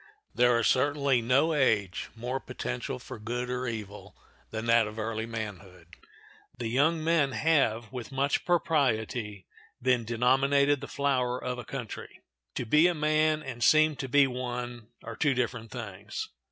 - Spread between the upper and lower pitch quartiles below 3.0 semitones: No, average, 3.9 semitones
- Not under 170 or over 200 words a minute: No, average, 155 wpm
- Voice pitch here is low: Yes, low, 125 Hz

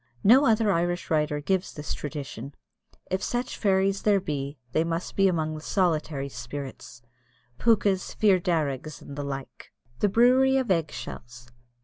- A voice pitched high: No, medium, 165 Hz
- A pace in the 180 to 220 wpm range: No, average, 150 wpm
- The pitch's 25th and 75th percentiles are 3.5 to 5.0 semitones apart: No, wide, 5.5 semitones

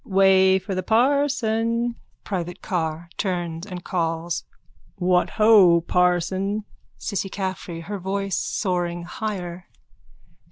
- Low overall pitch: No, high, 190 Hz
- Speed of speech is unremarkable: No, slow, 110 wpm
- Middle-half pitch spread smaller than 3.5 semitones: Yes, average, 2.9 semitones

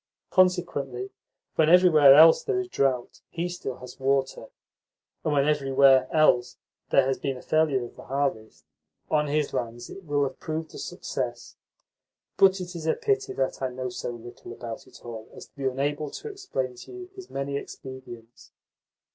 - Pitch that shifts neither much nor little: Yes, average, 4.0 semitones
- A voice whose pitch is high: No, medium, 140 Hz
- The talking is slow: No, average, 175 wpm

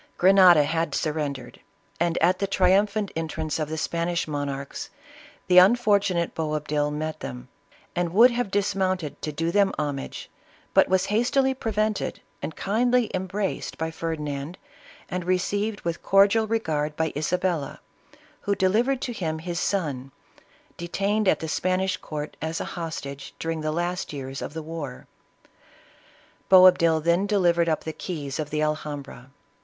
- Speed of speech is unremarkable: Yes, average, 150 wpm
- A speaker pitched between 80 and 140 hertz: No, medium, 170 Hz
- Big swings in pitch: No, average, 4.2 semitones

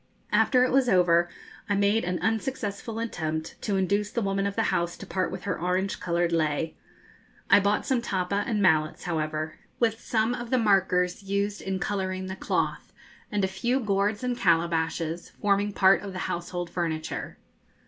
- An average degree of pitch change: Yes, average, 3.2 semitones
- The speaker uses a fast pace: No, average, 175 wpm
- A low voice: No, high, 195 Hz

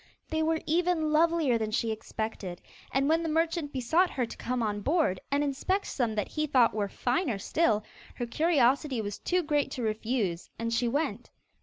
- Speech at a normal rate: Yes, average, 185 wpm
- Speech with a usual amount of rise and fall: No, wide, 6.1 semitones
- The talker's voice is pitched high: Yes, very high, 265 Hz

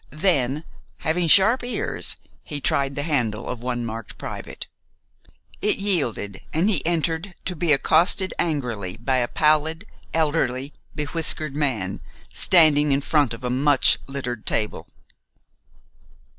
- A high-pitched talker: No, medium, 145 Hz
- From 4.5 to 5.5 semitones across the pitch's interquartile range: Yes, average, 4.8 semitones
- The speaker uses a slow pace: Yes, slow, 130 wpm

